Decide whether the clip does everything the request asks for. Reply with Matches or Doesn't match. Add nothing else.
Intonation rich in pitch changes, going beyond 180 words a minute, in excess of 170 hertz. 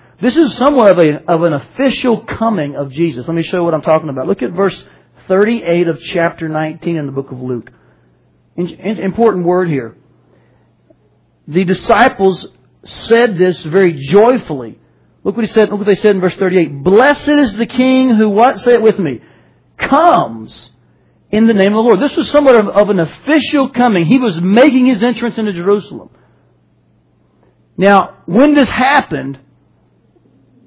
Doesn't match